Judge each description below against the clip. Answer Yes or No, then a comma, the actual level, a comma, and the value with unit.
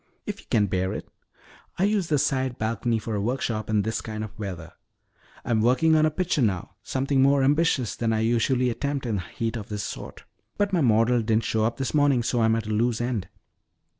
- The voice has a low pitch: Yes, low, 115 Hz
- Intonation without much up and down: No, average, 3.7 semitones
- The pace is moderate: No, fast, 215 wpm